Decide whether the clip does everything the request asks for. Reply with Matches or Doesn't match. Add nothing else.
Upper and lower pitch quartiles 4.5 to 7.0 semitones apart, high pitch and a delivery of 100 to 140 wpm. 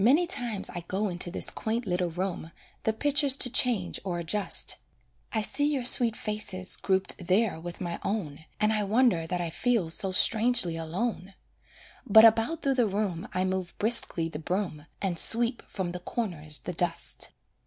Doesn't match